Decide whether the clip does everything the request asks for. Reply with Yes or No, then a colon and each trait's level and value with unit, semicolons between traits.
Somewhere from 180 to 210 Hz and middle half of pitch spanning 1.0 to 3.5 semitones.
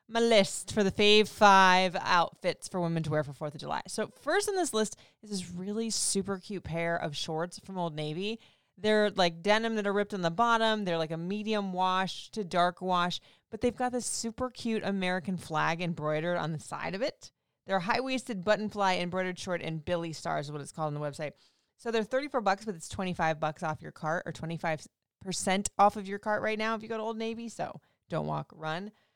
No: high, 190 Hz; average, 4.3 semitones